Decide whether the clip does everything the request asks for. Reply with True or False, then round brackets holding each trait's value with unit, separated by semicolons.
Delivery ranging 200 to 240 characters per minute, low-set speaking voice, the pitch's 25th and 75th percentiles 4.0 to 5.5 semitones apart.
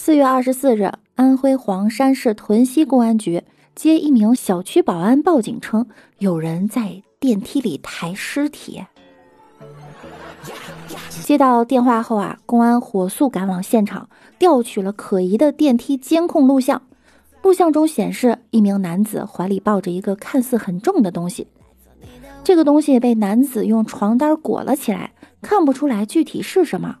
False (235 characters per minute; 240 Hz; 5.2 semitones)